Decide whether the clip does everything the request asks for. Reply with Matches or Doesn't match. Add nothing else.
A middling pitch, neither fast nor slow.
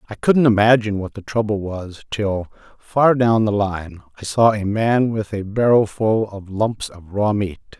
Doesn't match